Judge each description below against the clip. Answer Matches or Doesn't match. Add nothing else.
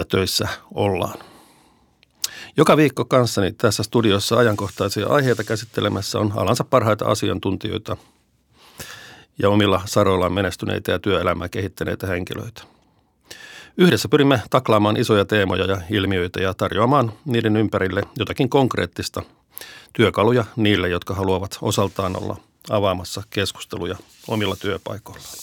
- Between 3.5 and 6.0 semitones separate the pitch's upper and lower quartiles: Doesn't match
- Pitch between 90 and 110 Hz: Matches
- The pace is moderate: Matches